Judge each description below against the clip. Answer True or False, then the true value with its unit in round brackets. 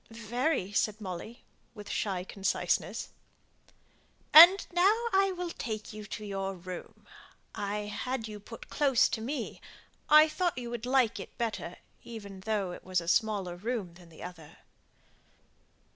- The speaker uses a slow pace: False (150 wpm)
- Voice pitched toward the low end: False (215 Hz)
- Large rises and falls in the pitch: False (4.7 semitones)